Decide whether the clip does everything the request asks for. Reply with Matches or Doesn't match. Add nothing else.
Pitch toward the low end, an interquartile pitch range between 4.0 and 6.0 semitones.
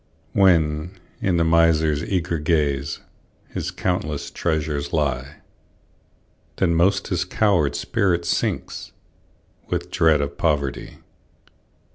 Doesn't match